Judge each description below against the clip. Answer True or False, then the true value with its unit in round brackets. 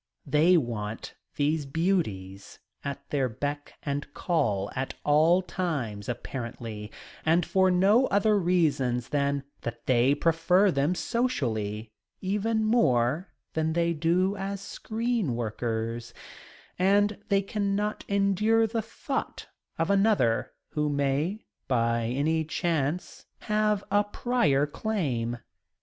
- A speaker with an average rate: False (115 wpm)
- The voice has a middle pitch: True (160 Hz)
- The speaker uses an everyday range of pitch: False (7.9 semitones)